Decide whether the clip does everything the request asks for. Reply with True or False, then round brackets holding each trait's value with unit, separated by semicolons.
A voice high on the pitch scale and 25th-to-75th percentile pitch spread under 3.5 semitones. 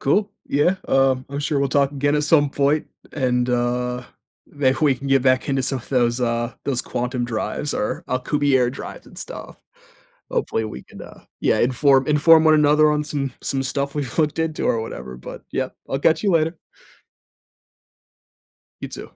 False (135 Hz; 3.0 semitones)